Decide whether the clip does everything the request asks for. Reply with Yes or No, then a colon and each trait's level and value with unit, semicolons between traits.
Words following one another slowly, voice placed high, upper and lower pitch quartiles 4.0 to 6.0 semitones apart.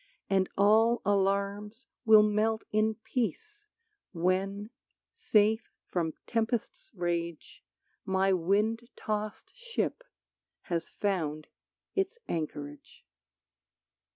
No: slow, 85 wpm; high, 205 Hz; average, 3.3 semitones